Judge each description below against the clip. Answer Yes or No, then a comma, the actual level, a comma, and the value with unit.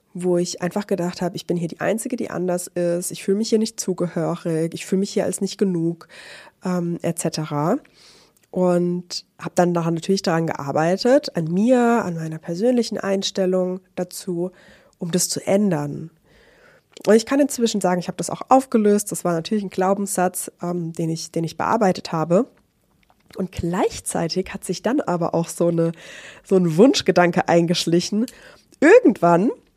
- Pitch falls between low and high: Yes, medium, 180 Hz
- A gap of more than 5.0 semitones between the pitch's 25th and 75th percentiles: No, average, 3.3 semitones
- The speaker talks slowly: No, average, 165 wpm